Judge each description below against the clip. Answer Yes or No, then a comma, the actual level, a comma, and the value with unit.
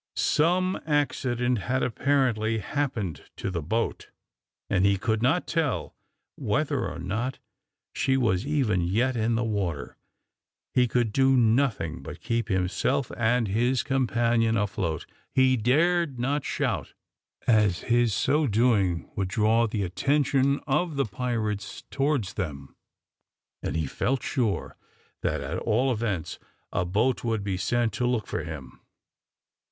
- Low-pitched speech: Yes, low, 115 Hz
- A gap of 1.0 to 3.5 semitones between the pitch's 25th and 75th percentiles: No, average, 4.7 semitones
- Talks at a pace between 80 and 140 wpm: Yes, slow, 135 wpm